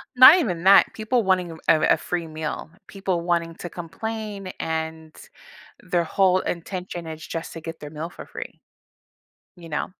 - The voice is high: No, medium, 175 Hz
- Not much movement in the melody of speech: No, average, 3.0 semitones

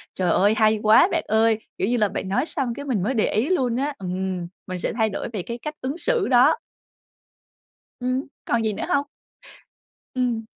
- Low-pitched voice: No, high, 235 Hz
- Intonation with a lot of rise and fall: No, average, 4.1 semitones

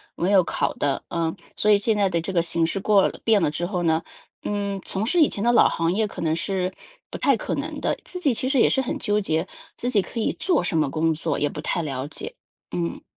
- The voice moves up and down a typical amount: Yes, average, 4.5 semitones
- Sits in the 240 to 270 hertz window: No, high, 190 Hz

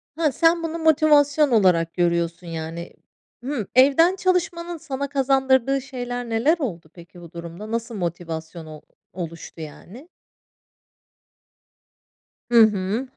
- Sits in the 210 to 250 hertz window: Yes, high, 240 Hz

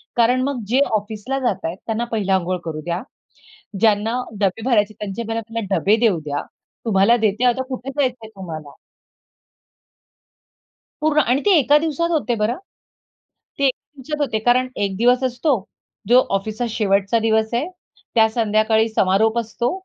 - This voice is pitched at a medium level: No, high, 225 Hz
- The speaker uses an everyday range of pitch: Yes, average, 3.5 semitones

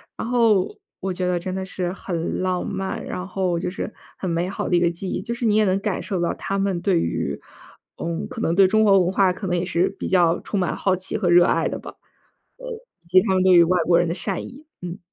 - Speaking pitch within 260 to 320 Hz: No, medium, 185 Hz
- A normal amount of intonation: No, narrow, 1.9 semitones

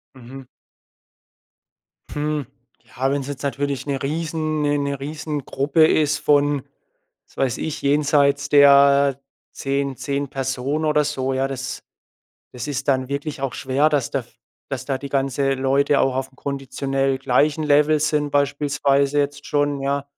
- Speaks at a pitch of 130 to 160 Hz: Yes, medium, 140 Hz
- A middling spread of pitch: No, narrow, 1.3 semitones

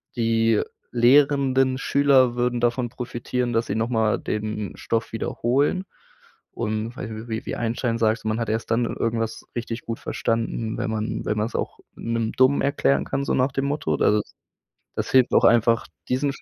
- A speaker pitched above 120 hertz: No, low, 115 Hz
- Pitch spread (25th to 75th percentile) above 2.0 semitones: Yes, narrow, 2.4 semitones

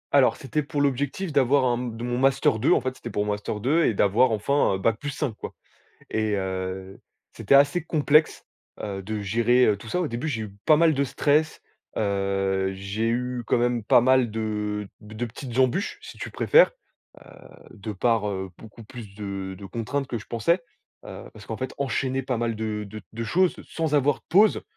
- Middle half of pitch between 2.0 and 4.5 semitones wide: No, average, 4.9 semitones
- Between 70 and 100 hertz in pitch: No, low, 115 Hz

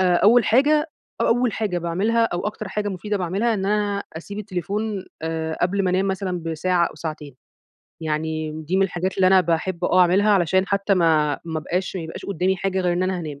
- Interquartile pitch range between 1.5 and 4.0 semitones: Yes, average, 3.2 semitones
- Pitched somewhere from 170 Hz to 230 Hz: Yes, medium, 185 Hz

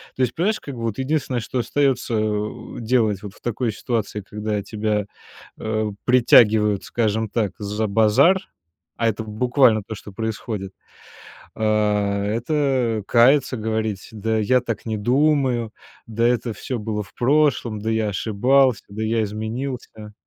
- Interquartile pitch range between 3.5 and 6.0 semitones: No, average, 2.9 semitones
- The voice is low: Yes, low, 110 Hz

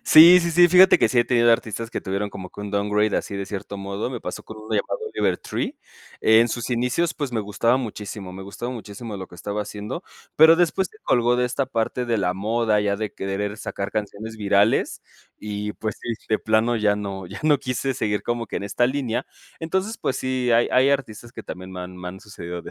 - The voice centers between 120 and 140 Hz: No, low, 110 Hz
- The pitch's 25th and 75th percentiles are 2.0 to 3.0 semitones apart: No, average, 3.5 semitones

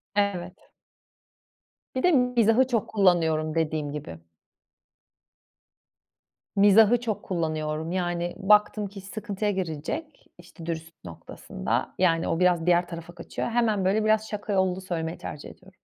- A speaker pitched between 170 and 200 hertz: Yes, medium, 185 Hz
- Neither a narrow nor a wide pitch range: Yes, average, 4.2 semitones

